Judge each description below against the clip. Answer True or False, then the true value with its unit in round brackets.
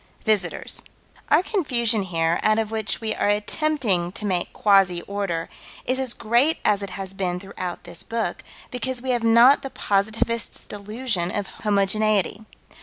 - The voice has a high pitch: True (210 Hz)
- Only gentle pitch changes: False (3.3 semitones)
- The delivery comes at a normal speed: True (155 wpm)